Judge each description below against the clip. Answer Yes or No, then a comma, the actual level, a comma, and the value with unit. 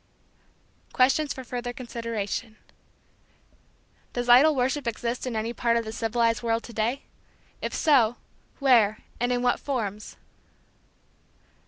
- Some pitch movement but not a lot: No, narrow, 1.9 semitones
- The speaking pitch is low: No, high, 240 Hz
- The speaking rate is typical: No, slow, 125 wpm